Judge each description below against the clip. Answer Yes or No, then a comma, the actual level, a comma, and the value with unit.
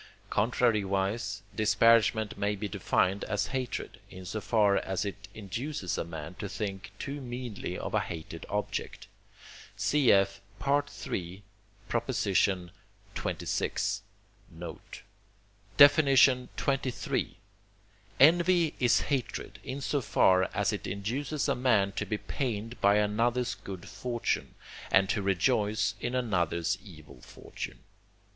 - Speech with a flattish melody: No, average, 4.5 semitones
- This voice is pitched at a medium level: No, low, 105 Hz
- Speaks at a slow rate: Yes, slow, 110 wpm